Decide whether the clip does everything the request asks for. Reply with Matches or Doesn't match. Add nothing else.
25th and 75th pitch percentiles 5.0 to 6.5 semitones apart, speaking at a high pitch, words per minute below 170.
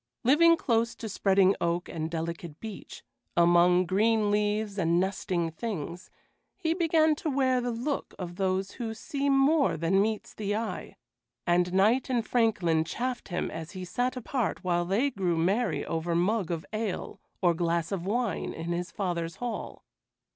Matches